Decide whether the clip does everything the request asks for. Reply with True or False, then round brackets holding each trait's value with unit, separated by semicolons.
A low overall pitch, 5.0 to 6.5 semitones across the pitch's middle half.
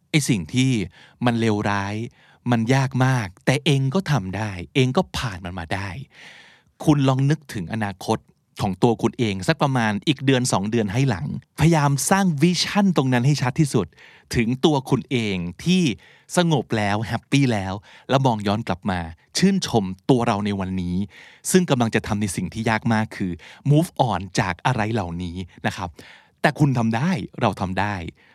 True (120 Hz; 5.6 semitones)